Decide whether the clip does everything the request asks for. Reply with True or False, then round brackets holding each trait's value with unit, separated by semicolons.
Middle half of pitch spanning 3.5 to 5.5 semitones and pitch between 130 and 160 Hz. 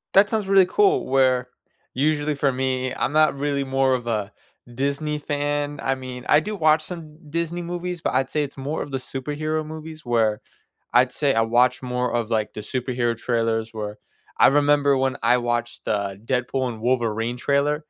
True (3.8 semitones; 135 Hz)